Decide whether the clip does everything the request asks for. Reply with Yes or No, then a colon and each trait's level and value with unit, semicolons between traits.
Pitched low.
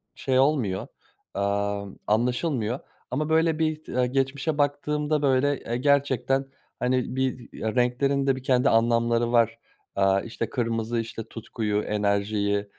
Yes: low, 125 Hz